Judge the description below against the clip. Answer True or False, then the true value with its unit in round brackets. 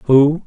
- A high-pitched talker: False (145 Hz)